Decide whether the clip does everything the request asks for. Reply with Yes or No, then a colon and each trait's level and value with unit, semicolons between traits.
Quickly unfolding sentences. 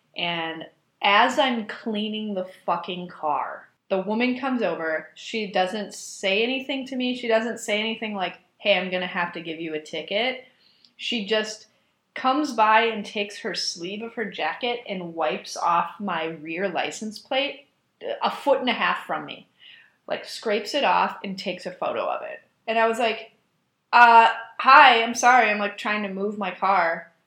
No: average, 180 wpm